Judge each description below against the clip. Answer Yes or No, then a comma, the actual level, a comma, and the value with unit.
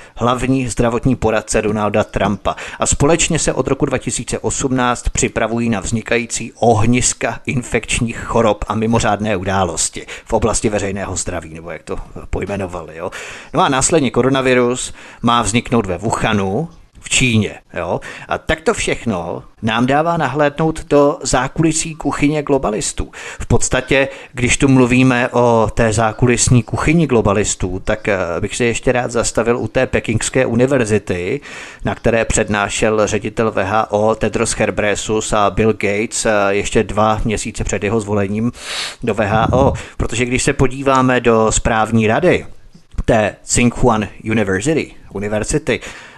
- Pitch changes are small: No, average, 3.0 semitones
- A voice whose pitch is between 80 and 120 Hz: Yes, low, 115 Hz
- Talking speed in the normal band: Yes, average, 130 wpm